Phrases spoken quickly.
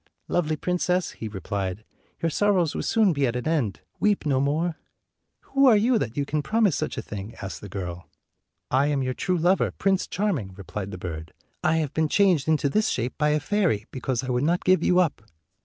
Yes: fast, 220 wpm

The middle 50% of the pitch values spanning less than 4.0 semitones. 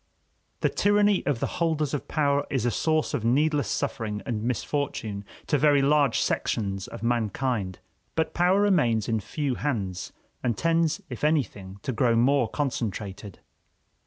No: wide, 5.4 semitones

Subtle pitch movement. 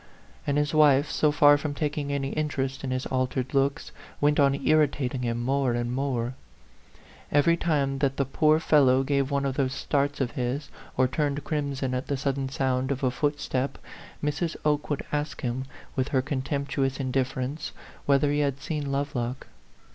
Yes: narrow, 1.9 semitones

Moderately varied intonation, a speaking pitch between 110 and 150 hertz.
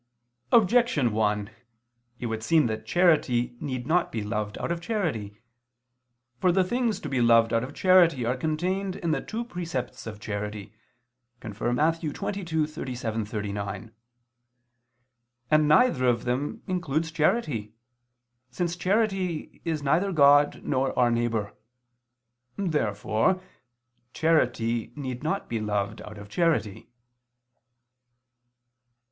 No: wide, 7.3 semitones; low, 135 Hz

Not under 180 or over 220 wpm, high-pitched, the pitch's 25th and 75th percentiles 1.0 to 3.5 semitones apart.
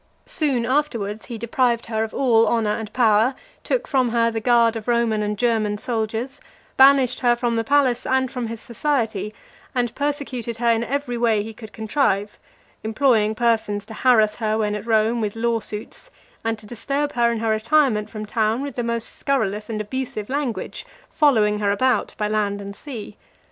Yes: average, 185 wpm; high, 230 Hz; average, 2.9 semitones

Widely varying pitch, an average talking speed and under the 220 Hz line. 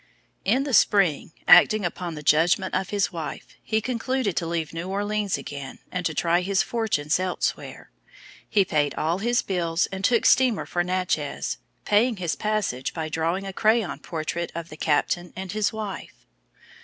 No: average, 4.3 semitones; average, 170 wpm; medium, 185 Hz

